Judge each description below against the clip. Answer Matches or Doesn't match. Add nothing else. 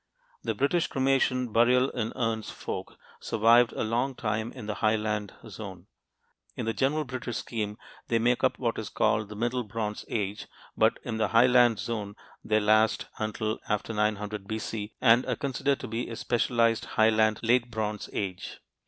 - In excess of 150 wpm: Matches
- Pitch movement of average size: Doesn't match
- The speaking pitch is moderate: Doesn't match